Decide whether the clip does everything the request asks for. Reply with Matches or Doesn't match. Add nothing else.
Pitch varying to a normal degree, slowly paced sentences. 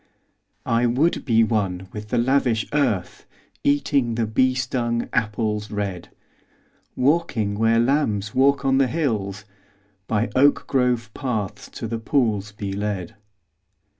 Matches